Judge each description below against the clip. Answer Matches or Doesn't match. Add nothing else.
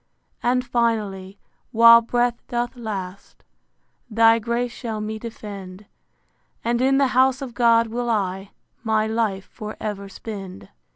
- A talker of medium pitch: Doesn't match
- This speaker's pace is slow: Matches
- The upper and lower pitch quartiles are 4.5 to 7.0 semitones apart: Doesn't match